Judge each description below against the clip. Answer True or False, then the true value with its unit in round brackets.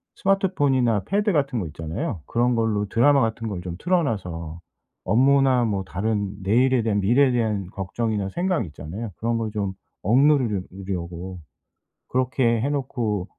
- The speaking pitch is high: False (115 Hz)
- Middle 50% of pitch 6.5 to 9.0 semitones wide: False (5.3 semitones)